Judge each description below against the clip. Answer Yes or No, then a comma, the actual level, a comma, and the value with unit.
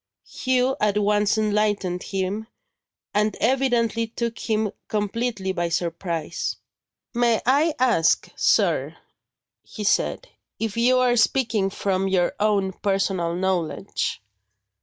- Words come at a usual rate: No, slow, 110 wpm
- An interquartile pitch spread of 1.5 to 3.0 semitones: No, average, 3.6 semitones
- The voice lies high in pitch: Yes, high, 210 Hz